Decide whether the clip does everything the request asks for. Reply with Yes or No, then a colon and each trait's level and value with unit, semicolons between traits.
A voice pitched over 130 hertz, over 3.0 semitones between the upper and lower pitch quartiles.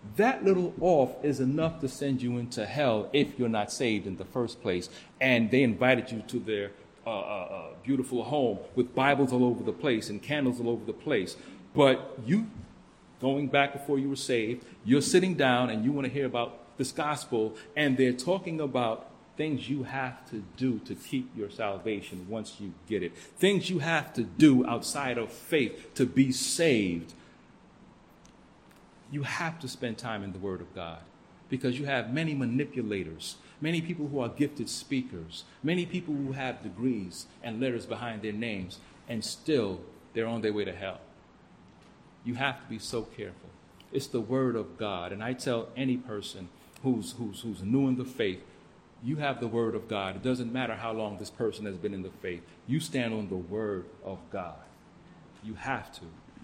No: low, 125 Hz; average, 4.3 semitones